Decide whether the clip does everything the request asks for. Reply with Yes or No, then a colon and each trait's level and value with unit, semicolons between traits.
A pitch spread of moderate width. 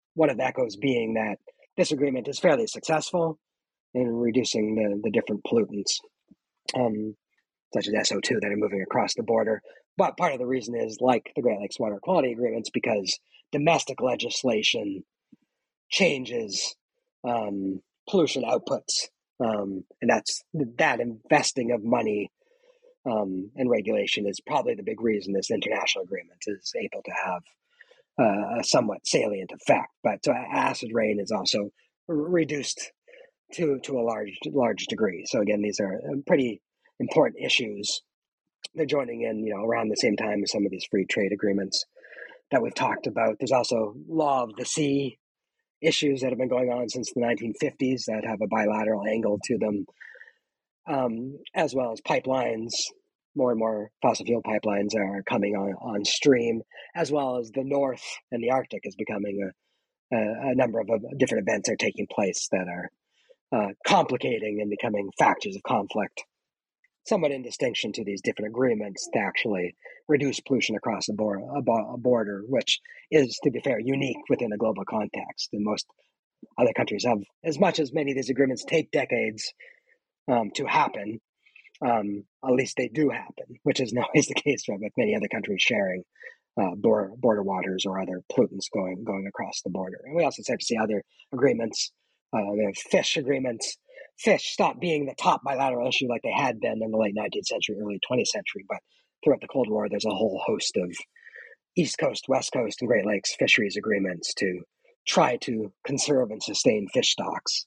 No: wide, 6.6 semitones